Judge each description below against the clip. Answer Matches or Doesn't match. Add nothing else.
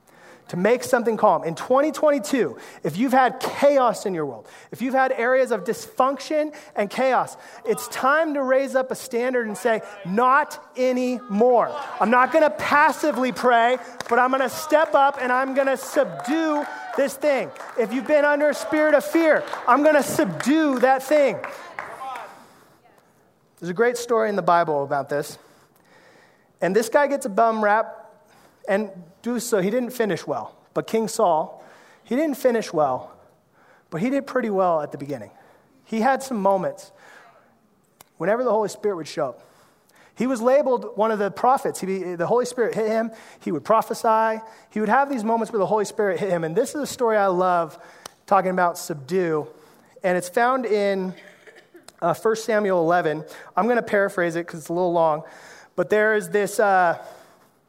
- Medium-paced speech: Matches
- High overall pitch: Matches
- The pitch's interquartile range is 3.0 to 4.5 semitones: Doesn't match